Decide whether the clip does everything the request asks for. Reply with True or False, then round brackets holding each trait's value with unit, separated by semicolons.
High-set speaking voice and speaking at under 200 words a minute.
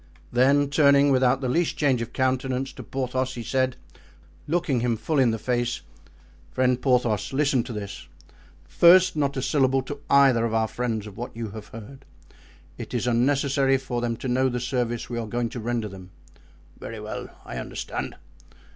False (125 Hz; 180 wpm)